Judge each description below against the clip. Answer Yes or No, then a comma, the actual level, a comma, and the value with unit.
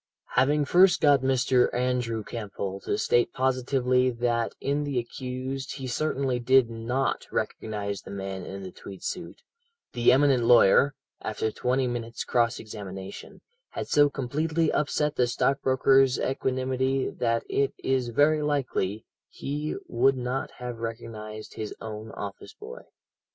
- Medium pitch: No, low, 125 Hz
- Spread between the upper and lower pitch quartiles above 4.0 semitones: No, average, 2.9 semitones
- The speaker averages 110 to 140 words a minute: Yes, slow, 135 wpm